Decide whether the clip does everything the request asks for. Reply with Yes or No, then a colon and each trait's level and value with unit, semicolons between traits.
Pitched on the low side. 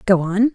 No: high, 205 Hz